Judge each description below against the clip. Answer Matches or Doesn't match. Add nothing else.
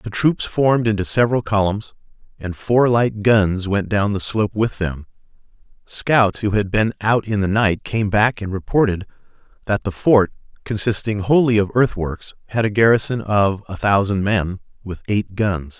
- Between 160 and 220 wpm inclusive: Matches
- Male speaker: Matches